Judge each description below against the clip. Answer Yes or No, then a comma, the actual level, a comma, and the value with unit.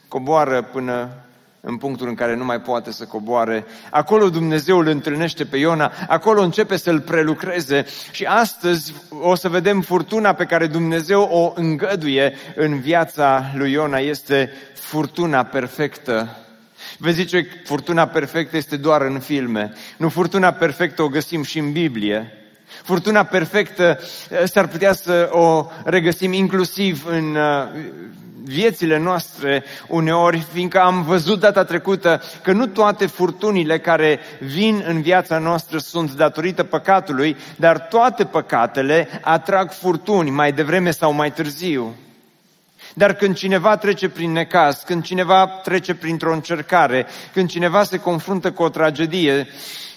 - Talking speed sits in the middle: Yes, average, 135 wpm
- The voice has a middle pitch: Yes, medium, 165 Hz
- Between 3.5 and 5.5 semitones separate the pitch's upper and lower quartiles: Yes, average, 3.8 semitones